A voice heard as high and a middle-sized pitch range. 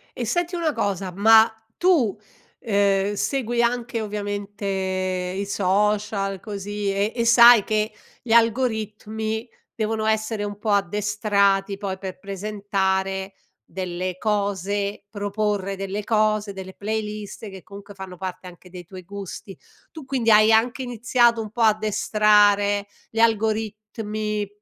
No: high, 205 Hz; narrow, 2.0 semitones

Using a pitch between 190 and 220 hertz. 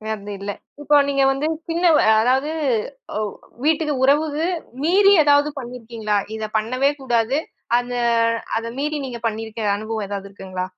No: high, 245 Hz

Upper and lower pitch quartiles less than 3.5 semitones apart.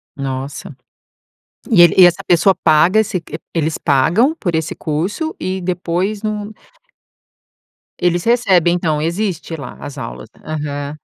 No: average, 4.1 semitones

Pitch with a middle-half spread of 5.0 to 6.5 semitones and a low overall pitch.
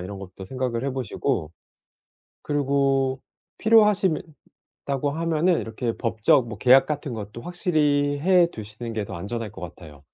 Yes: wide, 5.5 semitones; low, 130 Hz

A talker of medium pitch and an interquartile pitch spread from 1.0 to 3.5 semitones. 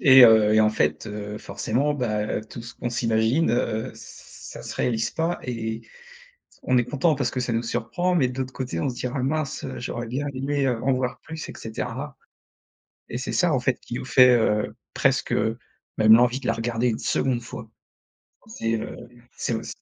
No: low, 120 Hz; average, 2.8 semitones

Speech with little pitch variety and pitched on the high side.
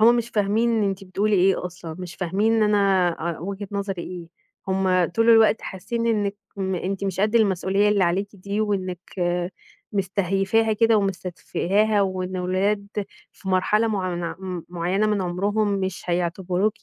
Yes: narrow, 2.3 semitones; high, 195 Hz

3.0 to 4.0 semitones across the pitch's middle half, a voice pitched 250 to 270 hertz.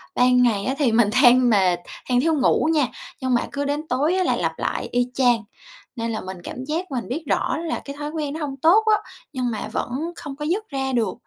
Yes: average, 3.7 semitones; very high, 265 Hz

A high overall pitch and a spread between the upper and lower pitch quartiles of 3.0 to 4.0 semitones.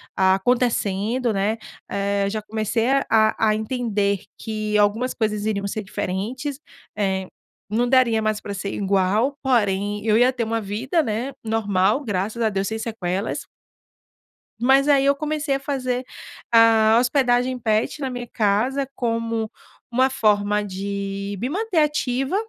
Yes: high, 220 Hz; average, 3.7 semitones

